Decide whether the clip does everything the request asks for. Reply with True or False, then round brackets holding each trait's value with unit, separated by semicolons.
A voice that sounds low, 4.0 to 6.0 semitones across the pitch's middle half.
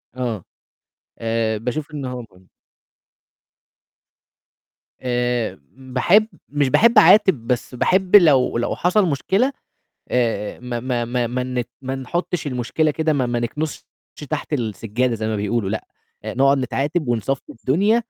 True (125 Hz; 4.3 semitones)